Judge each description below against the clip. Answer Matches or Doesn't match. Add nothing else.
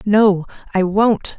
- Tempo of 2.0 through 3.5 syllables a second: Matches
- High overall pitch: Matches